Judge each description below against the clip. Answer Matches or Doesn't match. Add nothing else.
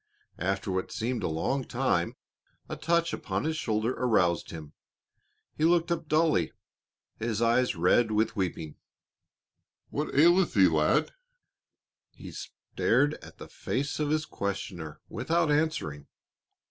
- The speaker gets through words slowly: Matches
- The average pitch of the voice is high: Doesn't match